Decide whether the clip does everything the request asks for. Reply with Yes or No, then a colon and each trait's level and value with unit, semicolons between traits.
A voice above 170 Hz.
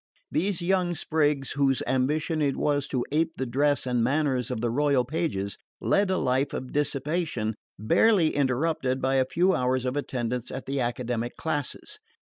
No: low, 135 Hz